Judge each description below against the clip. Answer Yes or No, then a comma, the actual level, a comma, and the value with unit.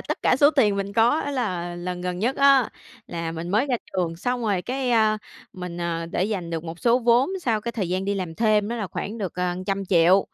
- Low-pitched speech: No, high, 200 Hz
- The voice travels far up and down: No, average, 5.0 semitones